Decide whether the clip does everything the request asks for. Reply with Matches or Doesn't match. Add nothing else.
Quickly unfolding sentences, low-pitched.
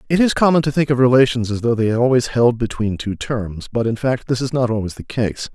Matches